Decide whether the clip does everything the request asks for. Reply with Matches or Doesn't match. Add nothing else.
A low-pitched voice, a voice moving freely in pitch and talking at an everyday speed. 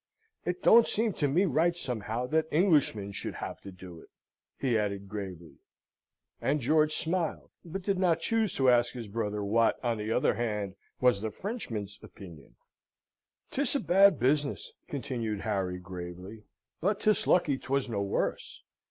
Matches